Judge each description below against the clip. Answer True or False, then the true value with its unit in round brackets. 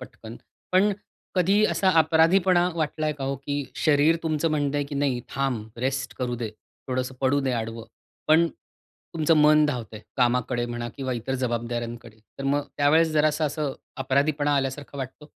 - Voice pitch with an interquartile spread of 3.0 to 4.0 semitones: True (3.5 semitones)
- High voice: False (140 Hz)